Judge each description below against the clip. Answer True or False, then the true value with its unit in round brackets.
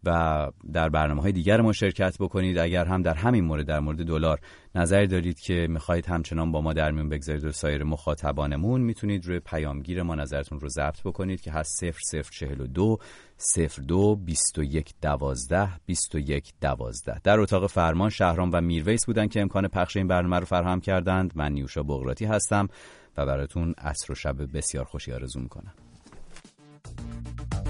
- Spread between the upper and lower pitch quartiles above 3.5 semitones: True (4.1 semitones)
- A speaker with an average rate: True (175 wpm)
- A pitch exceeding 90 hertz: False (85 Hz)